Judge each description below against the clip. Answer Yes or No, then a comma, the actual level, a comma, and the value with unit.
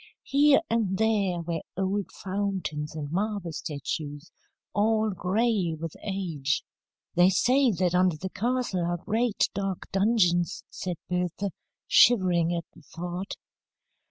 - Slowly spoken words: Yes, slow, 125 wpm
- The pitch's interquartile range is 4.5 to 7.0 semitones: No, average, 3.4 semitones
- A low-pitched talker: No, medium, 185 Hz